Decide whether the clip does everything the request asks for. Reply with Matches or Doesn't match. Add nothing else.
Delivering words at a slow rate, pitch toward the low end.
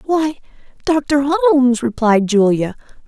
Doesn't match